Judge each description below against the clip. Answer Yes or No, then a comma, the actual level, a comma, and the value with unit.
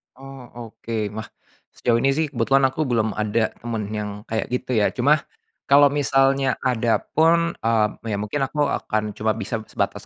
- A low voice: Yes, low, 120 Hz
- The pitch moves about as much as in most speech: Yes, average, 3.9 semitones